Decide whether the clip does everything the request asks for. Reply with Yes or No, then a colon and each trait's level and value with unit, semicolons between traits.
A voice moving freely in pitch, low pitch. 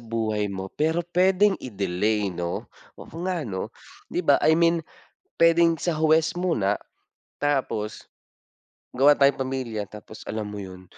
Yes: wide, 7.9 semitones; low, 130 Hz